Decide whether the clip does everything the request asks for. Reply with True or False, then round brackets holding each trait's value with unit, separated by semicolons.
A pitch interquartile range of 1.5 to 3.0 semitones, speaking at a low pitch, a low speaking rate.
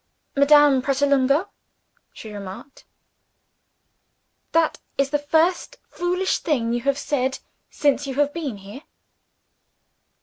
False (2.4 semitones; 280 Hz; 105 wpm)